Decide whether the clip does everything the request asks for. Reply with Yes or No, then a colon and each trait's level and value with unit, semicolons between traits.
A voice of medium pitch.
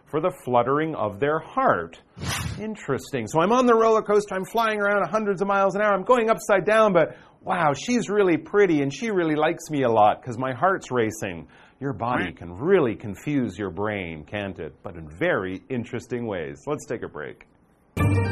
Yes: medium, 155 Hz